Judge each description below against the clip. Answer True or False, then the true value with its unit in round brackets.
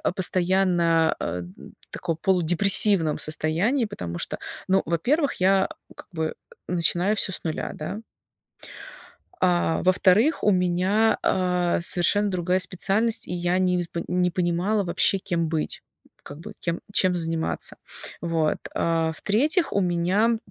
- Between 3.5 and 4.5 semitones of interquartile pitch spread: False (2.7 semitones)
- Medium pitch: True (180 Hz)